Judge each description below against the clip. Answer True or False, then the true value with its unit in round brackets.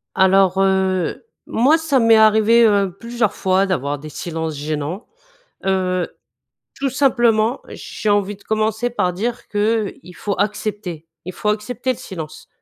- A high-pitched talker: True (205 Hz)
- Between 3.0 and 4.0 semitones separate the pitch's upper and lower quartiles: True (3.7 semitones)